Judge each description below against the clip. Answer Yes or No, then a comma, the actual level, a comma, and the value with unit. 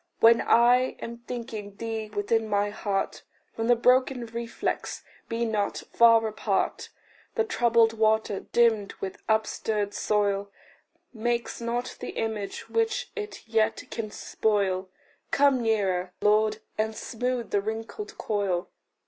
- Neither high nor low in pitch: No, high, 225 Hz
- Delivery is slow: Yes, slow, 125 wpm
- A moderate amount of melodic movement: No, narrow, 2.2 semitones